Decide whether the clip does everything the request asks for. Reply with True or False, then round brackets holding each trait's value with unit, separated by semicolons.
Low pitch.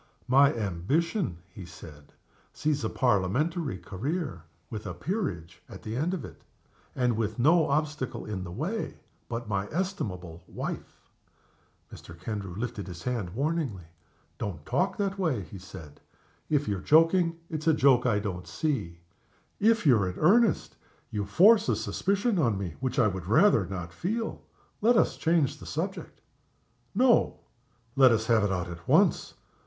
True (120 Hz)